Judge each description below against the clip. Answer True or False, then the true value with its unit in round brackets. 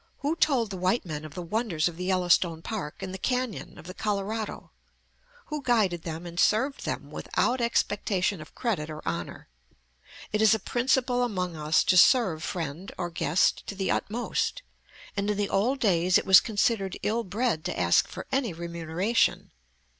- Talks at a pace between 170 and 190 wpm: True (175 wpm)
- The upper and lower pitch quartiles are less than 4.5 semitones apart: False (5.2 semitones)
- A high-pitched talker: True (195 Hz)